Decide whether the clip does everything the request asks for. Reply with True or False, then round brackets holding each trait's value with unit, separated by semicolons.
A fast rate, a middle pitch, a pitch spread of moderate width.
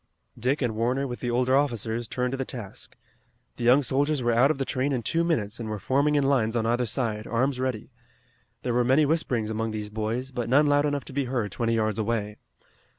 False (225 wpm; 125 Hz; 3.3 semitones)